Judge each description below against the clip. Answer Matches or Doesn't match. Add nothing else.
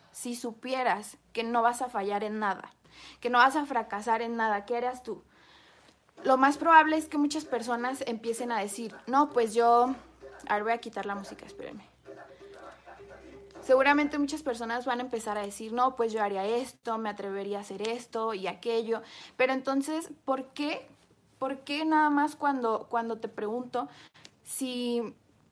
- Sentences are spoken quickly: Doesn't match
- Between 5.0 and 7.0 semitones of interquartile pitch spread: Doesn't match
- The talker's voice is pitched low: Doesn't match